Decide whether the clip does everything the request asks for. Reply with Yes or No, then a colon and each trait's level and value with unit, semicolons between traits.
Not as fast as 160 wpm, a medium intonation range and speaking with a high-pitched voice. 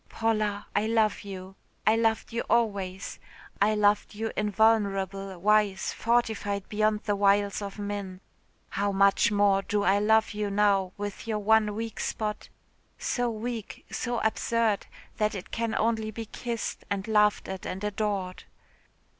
No: average, 145 wpm; narrow, 1.7 semitones; high, 210 Hz